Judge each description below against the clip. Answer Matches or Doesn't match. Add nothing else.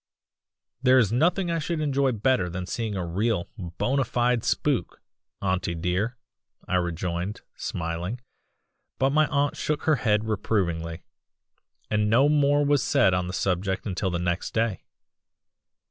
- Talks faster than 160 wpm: Doesn't match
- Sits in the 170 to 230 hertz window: Doesn't match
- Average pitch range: Doesn't match